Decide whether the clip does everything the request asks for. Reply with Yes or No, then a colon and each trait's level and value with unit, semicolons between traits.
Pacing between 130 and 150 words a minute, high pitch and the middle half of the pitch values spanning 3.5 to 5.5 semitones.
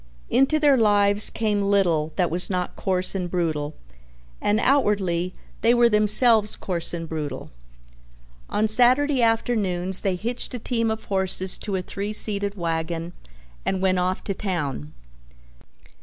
Yes: average, 140 wpm; high, 200 Hz; average, 3.8 semitones